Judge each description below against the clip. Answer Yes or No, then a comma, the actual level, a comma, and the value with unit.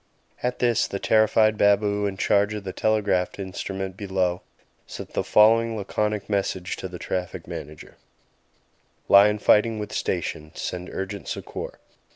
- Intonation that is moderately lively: No, narrow, 2.3 semitones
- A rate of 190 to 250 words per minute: No, average, 140 wpm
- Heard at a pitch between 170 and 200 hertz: No, low, 100 Hz